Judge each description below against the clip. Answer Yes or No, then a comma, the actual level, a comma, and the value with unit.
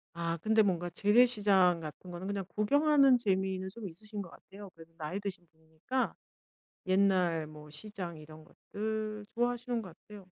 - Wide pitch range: No, average, 4.1 semitones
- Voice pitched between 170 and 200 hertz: Yes, high, 195 Hz